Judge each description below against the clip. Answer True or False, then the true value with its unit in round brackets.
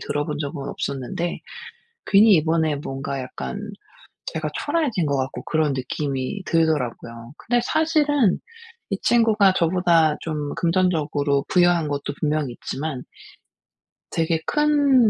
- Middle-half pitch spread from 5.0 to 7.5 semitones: True (5.6 semitones)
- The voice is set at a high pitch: False (160 Hz)